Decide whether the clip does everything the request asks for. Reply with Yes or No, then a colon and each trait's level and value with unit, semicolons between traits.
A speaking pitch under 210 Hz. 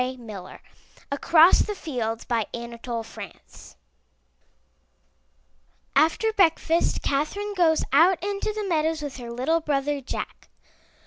No: very high, 305 Hz